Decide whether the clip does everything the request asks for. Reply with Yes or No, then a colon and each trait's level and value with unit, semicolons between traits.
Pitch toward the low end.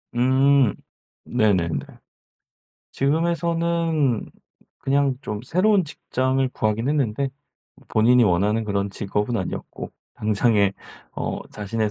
Yes: low, 125 Hz